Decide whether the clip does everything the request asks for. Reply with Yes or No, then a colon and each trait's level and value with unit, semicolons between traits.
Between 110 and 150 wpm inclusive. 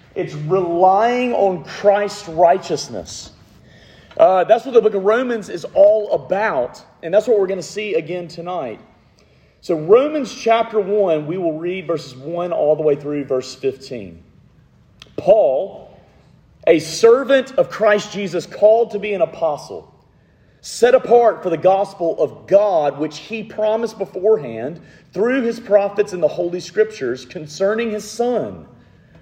Yes: average, 145 wpm